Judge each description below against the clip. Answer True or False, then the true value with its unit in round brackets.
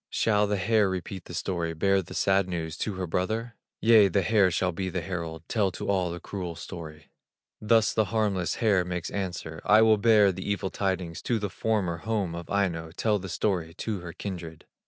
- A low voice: True (95 Hz)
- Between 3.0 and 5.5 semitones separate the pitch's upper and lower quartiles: True (3.3 semitones)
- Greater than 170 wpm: True (200 wpm)